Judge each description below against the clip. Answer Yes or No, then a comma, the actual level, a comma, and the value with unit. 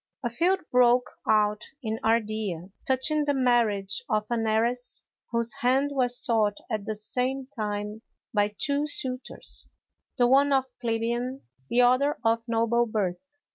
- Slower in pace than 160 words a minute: Yes, average, 145 wpm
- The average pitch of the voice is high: Yes, high, 235 Hz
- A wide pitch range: No, average, 3.2 semitones